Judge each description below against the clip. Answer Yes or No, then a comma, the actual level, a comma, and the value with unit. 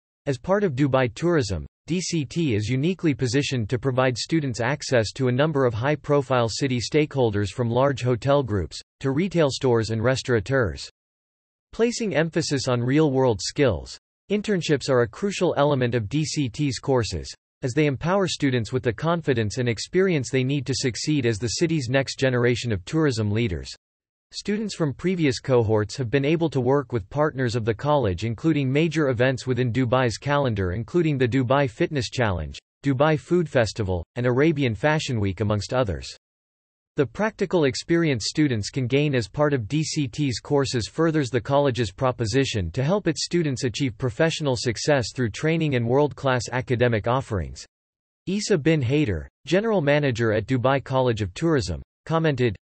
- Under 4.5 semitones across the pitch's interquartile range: Yes, average, 4.1 semitones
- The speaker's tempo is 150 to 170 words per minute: Yes, average, 160 wpm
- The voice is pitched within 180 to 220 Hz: No, low, 130 Hz